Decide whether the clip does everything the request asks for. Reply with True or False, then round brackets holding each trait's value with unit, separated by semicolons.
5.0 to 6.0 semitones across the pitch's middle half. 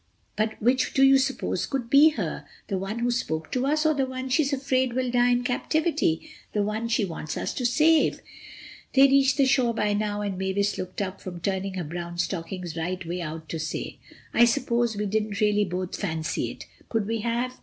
True (5.6 semitones)